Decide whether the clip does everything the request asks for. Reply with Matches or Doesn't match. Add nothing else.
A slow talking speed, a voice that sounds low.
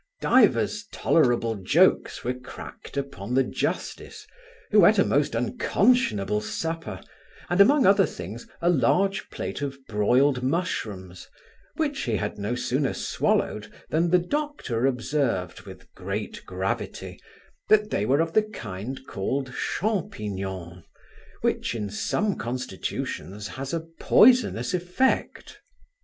Matches